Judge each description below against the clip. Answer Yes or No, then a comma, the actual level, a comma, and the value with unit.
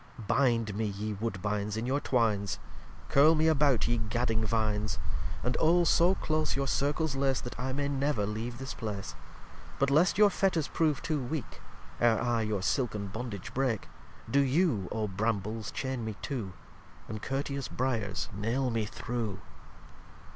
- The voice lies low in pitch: Yes, low, 120 Hz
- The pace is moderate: Yes, average, 160 wpm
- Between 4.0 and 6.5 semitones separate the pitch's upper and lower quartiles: Yes, average, 4.5 semitones